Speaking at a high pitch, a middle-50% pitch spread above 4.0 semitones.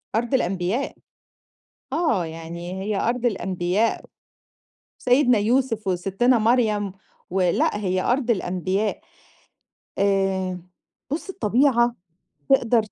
Yes: high, 210 Hz; average, 4.6 semitones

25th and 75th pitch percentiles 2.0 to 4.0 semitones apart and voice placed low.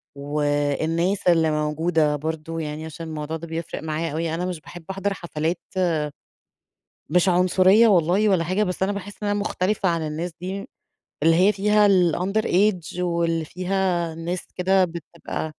No: average, 2.8 semitones; medium, 170 Hz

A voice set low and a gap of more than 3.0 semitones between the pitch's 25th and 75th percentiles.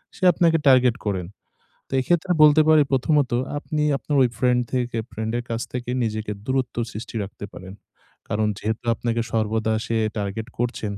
Yes: low, 120 Hz; average, 3.4 semitones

